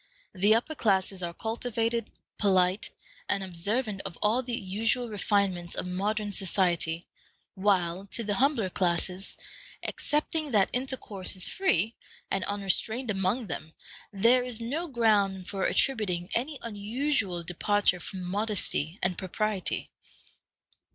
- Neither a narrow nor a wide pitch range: Yes, average, 3.8 semitones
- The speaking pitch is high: Yes, high, 205 Hz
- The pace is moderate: No, slow, 125 wpm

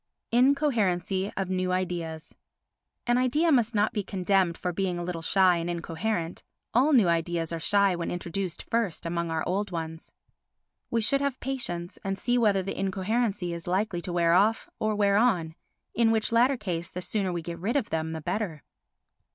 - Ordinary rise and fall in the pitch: Yes, average, 4.3 semitones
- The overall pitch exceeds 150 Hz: Yes, high, 190 Hz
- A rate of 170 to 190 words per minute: Yes, average, 185 wpm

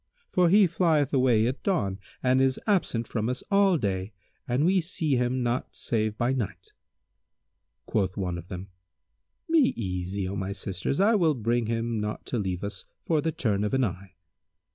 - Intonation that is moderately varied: No, wide, 7.1 semitones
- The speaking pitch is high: No, low, 120 Hz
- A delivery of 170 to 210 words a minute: Yes, average, 180 wpm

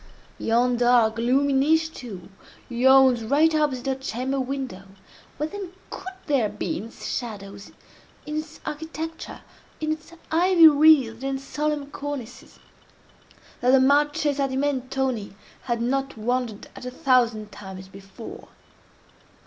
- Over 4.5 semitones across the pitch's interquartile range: No, average, 4.0 semitones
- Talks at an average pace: No, slow, 115 wpm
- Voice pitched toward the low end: No, very high, 265 Hz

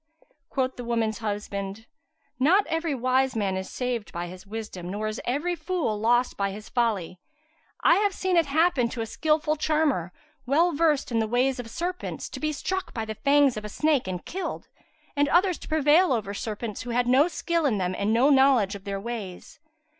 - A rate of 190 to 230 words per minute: Yes, average, 195 wpm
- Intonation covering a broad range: Yes, wide, 6.3 semitones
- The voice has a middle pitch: No, high, 245 Hz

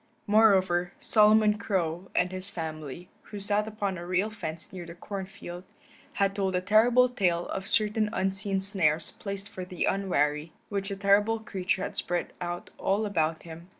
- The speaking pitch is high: Yes, high, 195 Hz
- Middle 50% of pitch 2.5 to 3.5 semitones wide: Yes, average, 2.9 semitones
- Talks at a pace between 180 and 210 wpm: No, average, 170 wpm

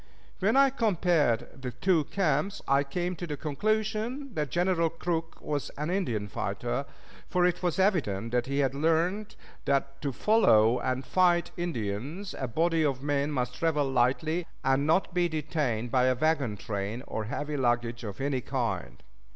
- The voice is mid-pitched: Yes, medium, 150 Hz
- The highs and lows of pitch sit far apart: Yes, wide, 5.7 semitones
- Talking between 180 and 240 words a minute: No, average, 165 wpm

